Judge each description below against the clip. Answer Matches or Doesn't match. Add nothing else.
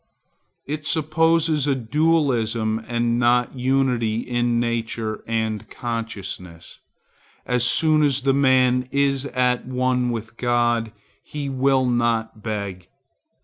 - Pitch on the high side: Doesn't match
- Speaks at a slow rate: Matches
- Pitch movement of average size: Matches